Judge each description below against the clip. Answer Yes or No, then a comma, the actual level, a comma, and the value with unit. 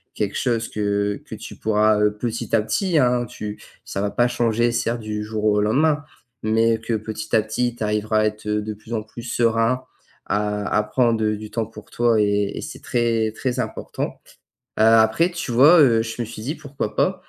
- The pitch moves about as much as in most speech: No, narrow, 2.0 semitones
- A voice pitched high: No, low, 110 Hz